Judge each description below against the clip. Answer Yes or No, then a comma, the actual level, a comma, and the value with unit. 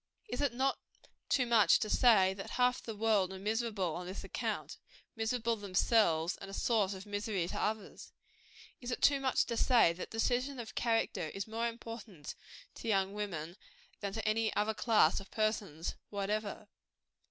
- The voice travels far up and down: No, average, 3.1 semitones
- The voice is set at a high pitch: Yes, high, 215 Hz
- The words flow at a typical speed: Yes, average, 165 wpm